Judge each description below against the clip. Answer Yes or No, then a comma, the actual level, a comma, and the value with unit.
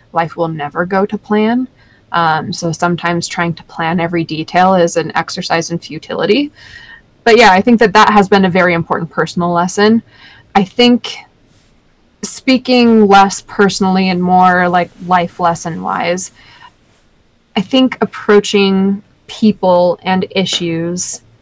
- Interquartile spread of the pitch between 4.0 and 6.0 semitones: No, average, 3.3 semitones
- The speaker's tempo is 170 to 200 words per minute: No, slow, 135 wpm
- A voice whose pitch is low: No, medium, 185 Hz